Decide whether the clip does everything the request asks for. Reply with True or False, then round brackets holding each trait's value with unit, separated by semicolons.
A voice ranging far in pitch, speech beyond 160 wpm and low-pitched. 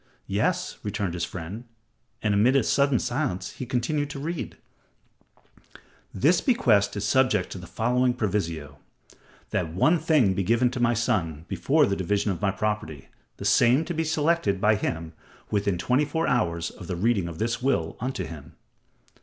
True (6.3 semitones; 170 wpm; 110 Hz)